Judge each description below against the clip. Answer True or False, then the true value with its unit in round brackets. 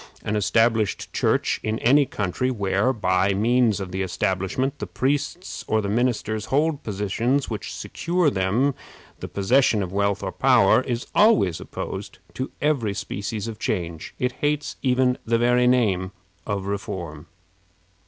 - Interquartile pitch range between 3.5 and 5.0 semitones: True (4.6 semitones)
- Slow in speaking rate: False (150 wpm)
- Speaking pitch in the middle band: False (110 Hz)